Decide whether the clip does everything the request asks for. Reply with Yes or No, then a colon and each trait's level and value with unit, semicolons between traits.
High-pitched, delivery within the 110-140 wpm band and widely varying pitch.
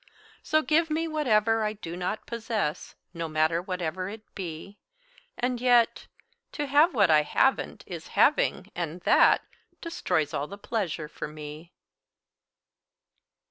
Yes: high, 200 Hz; slow, 135 wpm; wide, 7.0 semitones